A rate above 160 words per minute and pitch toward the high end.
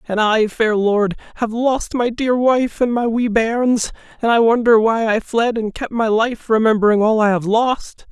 Yes: fast, 205 wpm; high, 225 Hz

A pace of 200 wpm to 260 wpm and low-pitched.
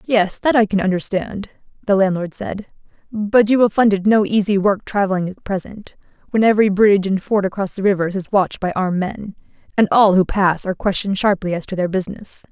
No: fast, 205 wpm; high, 200 Hz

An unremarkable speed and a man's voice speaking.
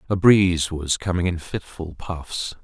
Yes: average, 160 wpm; male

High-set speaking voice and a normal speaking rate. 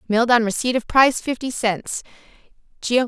Yes: high, 235 Hz; average, 155 wpm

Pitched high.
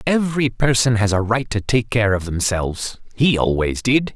No: low, 115 Hz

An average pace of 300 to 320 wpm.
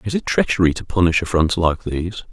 No: fast, 205 wpm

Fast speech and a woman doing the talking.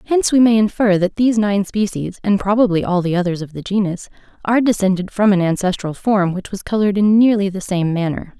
Yes: fast, 215 wpm; female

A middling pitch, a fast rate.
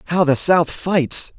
No: medium, 160 Hz; average, 175 wpm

